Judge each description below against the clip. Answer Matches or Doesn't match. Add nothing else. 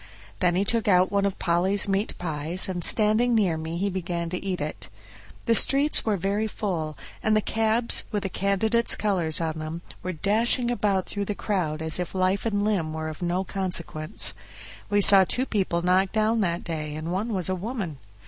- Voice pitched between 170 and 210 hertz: Matches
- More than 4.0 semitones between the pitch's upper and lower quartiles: Doesn't match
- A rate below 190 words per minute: Doesn't match